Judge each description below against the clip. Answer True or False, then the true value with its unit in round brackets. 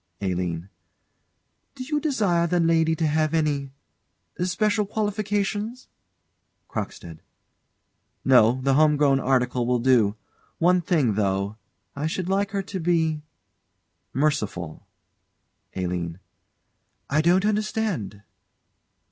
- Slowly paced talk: True (105 wpm)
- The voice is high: False (155 Hz)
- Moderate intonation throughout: False (8.2 semitones)